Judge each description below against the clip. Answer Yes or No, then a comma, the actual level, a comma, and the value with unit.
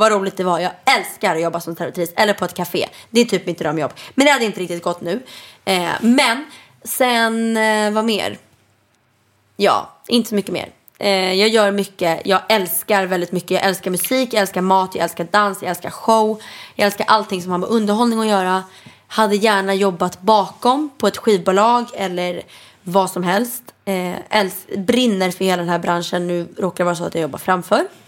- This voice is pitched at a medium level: No, high, 195 Hz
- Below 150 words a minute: No, average, 195 wpm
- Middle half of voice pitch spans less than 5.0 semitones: Yes, average, 3.5 semitones